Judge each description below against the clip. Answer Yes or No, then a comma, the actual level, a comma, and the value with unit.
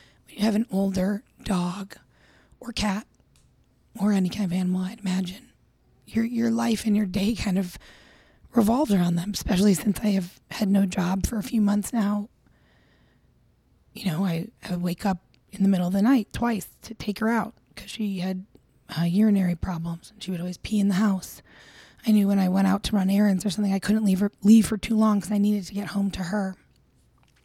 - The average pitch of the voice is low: No, high, 200 Hz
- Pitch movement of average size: No, narrow, 2.3 semitones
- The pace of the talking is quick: Yes, fast, 210 wpm